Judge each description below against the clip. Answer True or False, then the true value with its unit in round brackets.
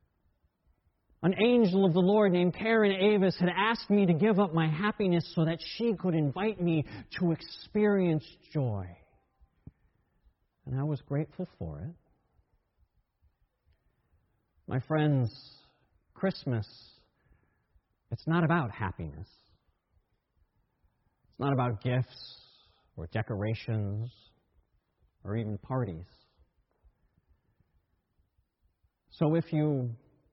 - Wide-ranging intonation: True (9.0 semitones)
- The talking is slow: True (100 wpm)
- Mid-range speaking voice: False (130 Hz)